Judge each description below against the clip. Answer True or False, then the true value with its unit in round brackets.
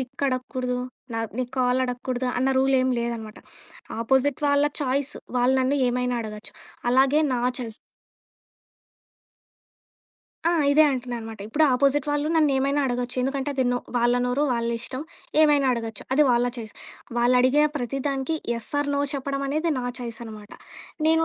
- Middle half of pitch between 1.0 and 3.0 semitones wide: True (2.4 semitones)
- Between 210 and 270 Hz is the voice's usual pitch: True (255 Hz)